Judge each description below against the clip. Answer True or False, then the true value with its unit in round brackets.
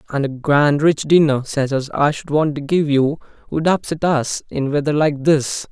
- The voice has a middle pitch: True (145 Hz)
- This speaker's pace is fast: True (210 wpm)